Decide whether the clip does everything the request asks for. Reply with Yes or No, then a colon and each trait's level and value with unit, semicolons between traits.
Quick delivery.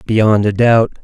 No: average, 175 wpm